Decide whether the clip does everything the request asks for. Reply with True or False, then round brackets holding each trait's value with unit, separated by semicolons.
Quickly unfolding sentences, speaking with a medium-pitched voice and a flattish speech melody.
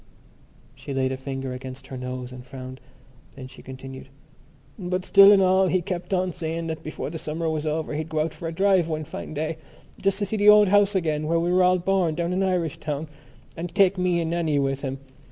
False (225 wpm; 160 Hz; 4.7 semitones)